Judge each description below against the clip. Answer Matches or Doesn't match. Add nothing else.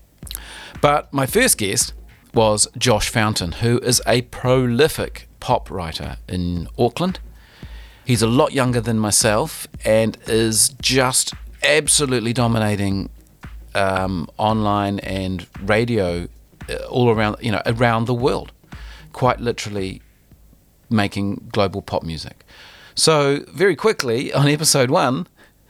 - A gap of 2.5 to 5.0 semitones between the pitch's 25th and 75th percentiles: Matches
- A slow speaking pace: Matches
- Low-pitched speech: Matches